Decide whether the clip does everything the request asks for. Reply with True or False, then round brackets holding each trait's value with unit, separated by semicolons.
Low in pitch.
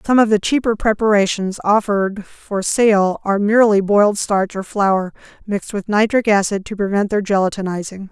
False (205 Hz)